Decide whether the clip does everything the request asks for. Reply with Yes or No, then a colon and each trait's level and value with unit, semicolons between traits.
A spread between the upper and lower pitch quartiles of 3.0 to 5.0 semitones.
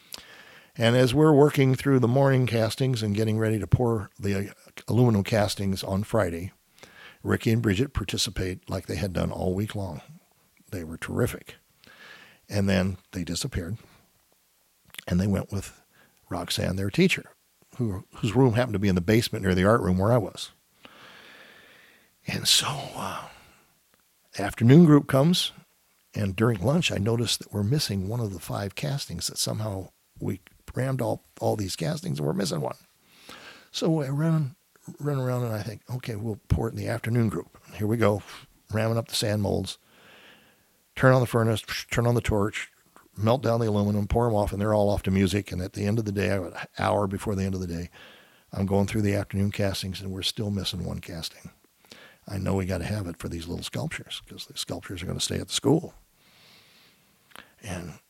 Yes: average, 3.7 semitones